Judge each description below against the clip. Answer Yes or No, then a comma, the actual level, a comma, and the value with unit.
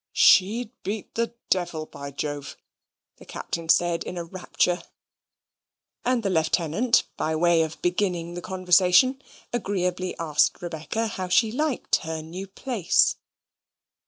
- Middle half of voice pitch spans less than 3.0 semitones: No, average, 3.8 semitones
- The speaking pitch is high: No, medium, 180 Hz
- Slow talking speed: Yes, slow, 130 wpm